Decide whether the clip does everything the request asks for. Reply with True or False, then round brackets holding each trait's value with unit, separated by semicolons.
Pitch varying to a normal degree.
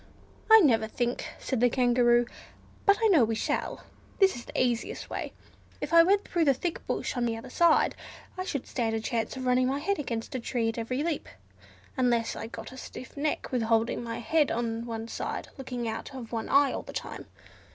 True (3.8 semitones)